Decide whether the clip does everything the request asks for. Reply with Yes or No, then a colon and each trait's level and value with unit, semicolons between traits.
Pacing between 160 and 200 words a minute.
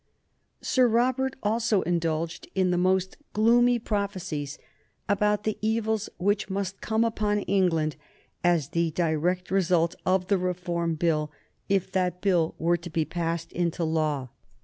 No: average, 140 wpm